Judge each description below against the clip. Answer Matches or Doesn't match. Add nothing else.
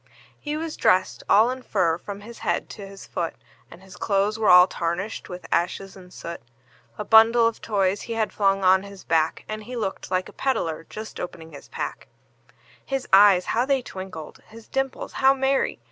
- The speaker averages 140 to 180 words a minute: Doesn't match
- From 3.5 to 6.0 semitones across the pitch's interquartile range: Matches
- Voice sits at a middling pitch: Doesn't match